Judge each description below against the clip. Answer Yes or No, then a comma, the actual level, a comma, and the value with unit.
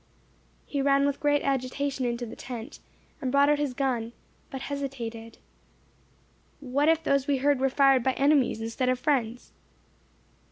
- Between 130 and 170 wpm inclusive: Yes, average, 155 wpm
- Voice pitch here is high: Yes, very high, 270 Hz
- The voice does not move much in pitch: Yes, narrow, 2.3 semitones